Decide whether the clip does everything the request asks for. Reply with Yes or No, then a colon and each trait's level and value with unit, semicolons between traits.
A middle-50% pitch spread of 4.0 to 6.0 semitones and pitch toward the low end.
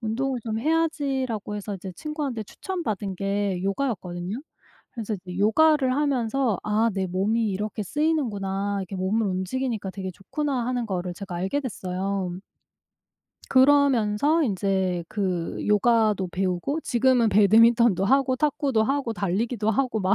No: average, 5.2 semitones; high, 215 Hz